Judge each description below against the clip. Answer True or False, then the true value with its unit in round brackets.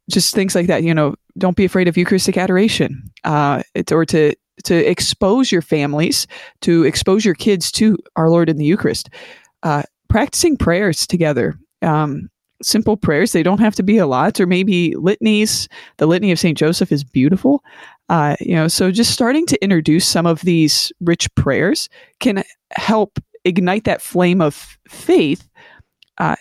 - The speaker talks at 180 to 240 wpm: False (170 wpm)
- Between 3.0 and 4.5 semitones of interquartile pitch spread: False (4.9 semitones)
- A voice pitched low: False (185 Hz)